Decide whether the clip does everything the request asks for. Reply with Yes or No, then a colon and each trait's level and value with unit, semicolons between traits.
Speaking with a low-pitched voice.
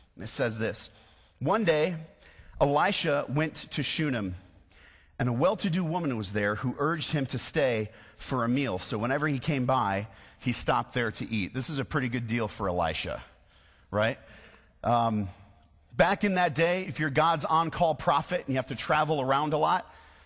Yes: low, 130 Hz